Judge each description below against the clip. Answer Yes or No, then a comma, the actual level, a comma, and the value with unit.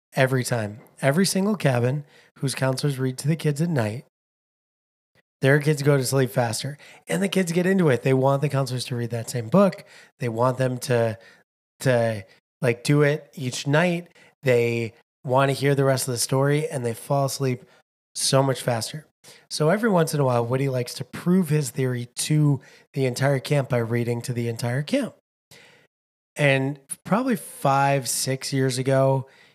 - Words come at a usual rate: Yes, average, 180 wpm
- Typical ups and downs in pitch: Yes, average, 3.2 semitones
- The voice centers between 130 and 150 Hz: Yes, low, 135 Hz